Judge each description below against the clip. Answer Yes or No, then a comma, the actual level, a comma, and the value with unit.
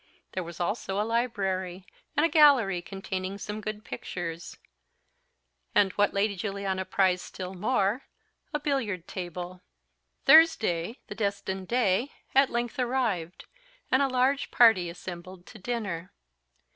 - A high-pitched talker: Yes, high, 200 Hz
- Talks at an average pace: No, slow, 130 wpm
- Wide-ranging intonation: No, average, 4.6 semitones